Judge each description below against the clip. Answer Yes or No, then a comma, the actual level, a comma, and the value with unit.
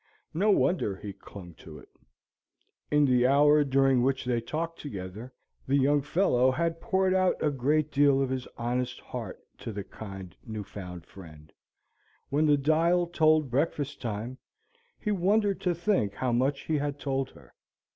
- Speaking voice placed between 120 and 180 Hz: Yes, low, 135 Hz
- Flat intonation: No, average, 4.8 semitones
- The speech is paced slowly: No, average, 165 wpm